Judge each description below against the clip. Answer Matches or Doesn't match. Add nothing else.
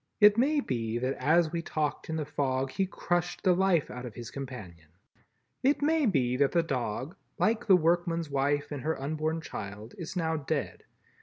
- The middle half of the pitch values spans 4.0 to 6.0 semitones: Matches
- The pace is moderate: Matches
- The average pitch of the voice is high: Doesn't match